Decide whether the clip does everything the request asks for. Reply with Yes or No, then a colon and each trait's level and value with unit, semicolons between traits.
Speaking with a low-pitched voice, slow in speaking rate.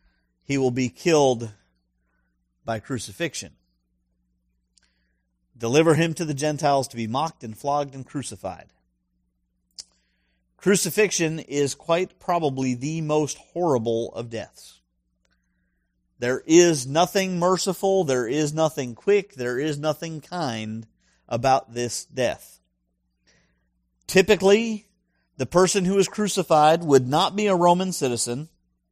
Yes: low, 130 Hz; slow, 110 wpm